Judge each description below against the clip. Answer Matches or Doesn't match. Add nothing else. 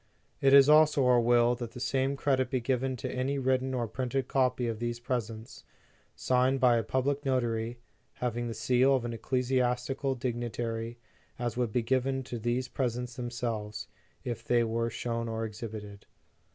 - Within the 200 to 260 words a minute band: Doesn't match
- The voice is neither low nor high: Doesn't match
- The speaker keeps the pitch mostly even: Matches